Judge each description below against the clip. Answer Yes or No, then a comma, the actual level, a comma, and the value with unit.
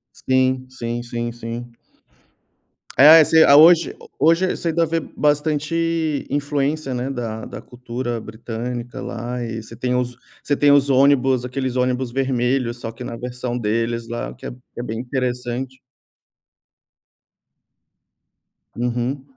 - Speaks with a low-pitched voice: Yes, low, 125 Hz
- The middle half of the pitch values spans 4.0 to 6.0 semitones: No, average, 2.9 semitones